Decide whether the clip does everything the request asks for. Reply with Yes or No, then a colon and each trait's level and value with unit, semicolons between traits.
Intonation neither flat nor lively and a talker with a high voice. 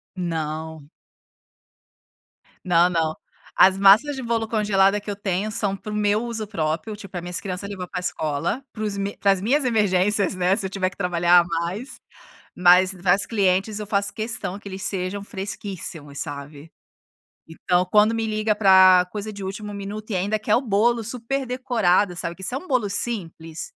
Yes: average, 3.1 semitones; high, 195 Hz